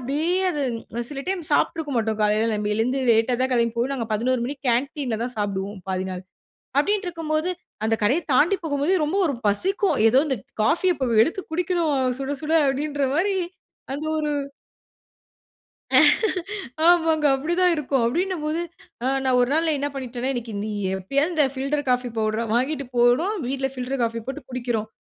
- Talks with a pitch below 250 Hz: No, very high, 270 Hz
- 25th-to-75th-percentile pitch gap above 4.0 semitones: Yes, average, 4.7 semitones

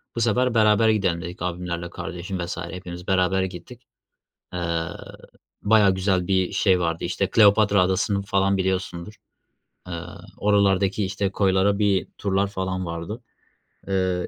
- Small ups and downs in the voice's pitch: Yes, narrow, 2.1 semitones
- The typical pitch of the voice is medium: No, very low, 95 Hz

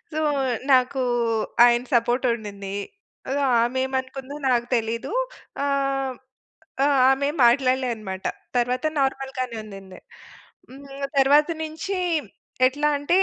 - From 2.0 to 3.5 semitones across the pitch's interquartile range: Yes, average, 2.8 semitones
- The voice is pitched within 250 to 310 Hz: Yes, very high, 260 Hz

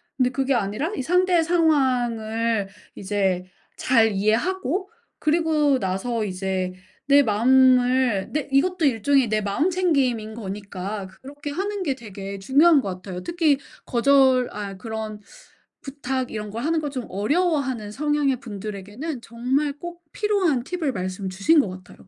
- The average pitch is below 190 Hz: No, very high, 255 Hz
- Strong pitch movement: Yes, wide, 6.0 semitones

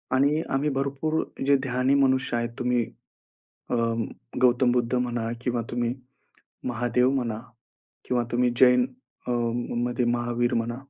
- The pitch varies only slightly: Yes, narrow, 1.6 semitones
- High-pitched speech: No, low, 125 Hz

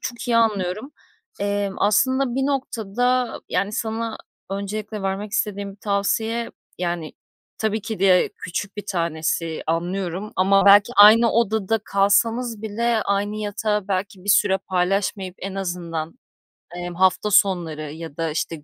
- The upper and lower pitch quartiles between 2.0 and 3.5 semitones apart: Yes, average, 3.1 semitones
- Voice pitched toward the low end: No, high, 200 Hz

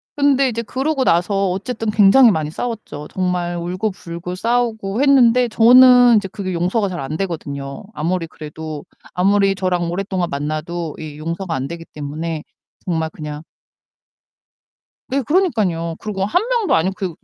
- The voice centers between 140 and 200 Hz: Yes, medium, 185 Hz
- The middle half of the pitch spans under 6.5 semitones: Yes, wide, 5.6 semitones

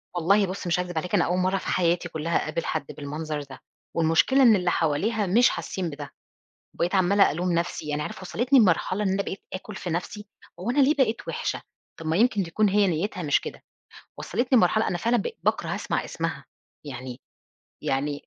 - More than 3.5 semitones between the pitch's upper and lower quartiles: Yes, average, 4.5 semitones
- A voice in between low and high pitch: Yes, medium, 180 Hz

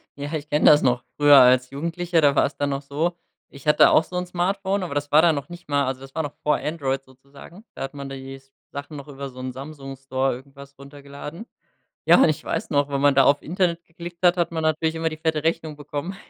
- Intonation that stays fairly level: No, average, 3.0 semitones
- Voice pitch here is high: No, medium, 145 Hz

